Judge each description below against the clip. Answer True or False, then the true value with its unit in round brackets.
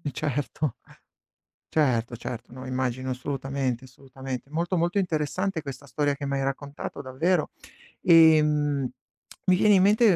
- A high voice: False (140 Hz)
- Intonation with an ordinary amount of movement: True (3.8 semitones)